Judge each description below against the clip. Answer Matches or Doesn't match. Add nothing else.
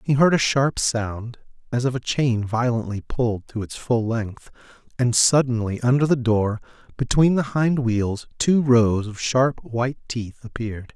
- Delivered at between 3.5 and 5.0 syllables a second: Matches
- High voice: Doesn't match